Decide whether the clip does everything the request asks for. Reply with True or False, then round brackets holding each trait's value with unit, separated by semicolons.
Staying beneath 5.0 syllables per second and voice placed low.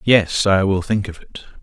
True (4.4 syllables/s; 100 Hz)